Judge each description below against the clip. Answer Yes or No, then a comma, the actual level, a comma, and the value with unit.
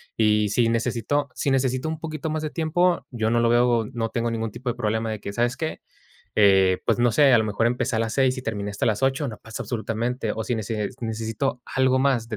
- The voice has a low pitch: Yes, low, 120 Hz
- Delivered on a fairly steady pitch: No, average, 3.0 semitones